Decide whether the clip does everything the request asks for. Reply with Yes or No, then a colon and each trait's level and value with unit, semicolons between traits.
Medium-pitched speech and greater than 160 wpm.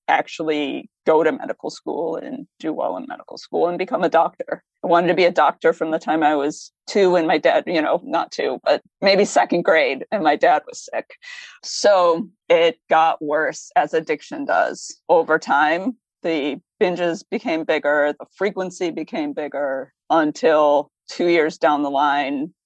Yes: medium, 175 Hz; average, 175 wpm